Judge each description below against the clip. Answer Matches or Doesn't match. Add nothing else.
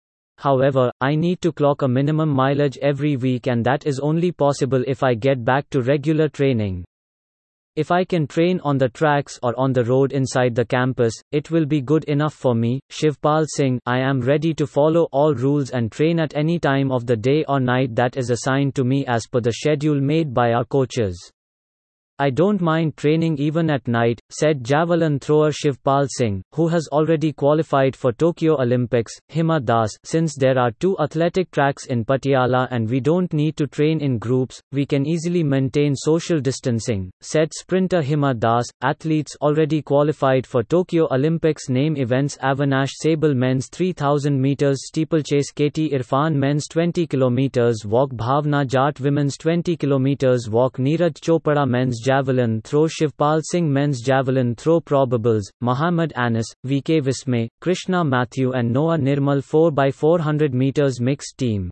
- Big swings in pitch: Doesn't match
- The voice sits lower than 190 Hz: Matches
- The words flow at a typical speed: Matches